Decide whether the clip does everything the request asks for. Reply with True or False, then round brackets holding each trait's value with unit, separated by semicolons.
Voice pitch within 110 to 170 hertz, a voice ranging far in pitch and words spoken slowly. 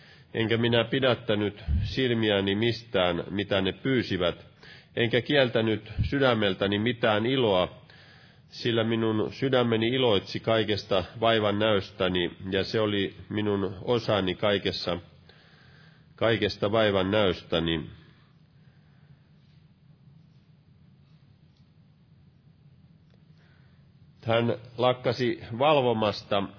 True (115 Hz; 6.0 semitones; 70 wpm)